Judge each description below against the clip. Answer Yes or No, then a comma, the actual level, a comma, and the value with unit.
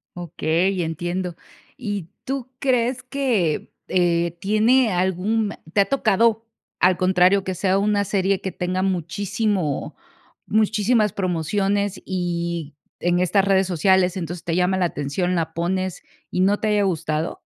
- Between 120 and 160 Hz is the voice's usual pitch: No, high, 190 Hz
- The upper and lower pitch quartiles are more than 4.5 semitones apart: No, average, 2.8 semitones